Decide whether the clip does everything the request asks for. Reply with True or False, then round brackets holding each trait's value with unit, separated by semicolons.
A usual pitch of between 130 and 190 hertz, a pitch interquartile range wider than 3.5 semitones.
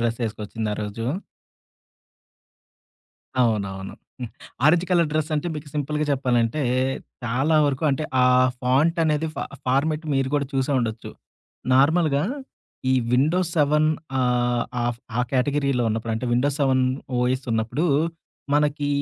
True (135 Hz; 4.0 semitones)